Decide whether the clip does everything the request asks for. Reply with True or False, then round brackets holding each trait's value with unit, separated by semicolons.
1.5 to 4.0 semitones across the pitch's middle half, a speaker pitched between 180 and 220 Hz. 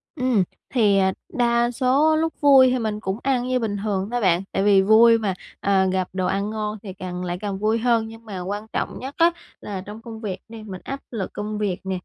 True (3.7 semitones; 215 Hz)